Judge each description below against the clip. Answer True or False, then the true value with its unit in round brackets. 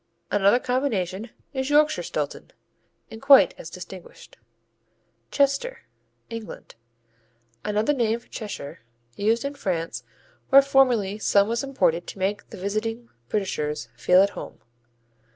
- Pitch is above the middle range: True (220 Hz)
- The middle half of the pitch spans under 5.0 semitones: False (5.5 semitones)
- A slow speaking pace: True (120 wpm)